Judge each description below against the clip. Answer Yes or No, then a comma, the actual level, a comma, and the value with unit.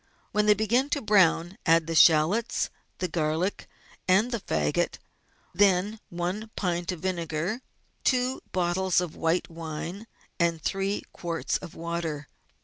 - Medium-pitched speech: Yes, medium, 180 Hz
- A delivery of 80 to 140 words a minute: Yes, slow, 135 wpm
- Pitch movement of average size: Yes, average, 3.8 semitones